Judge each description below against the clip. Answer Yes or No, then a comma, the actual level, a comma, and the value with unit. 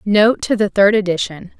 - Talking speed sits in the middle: Yes, average, 190 wpm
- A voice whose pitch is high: Yes, high, 200 Hz